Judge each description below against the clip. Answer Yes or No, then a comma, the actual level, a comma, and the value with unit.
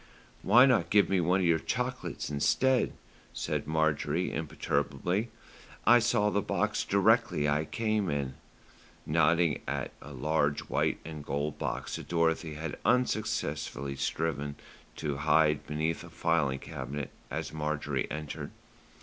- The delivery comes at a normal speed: No, slow, 130 wpm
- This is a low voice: Yes, very low, 80 Hz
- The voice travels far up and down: No, average, 3.4 semitones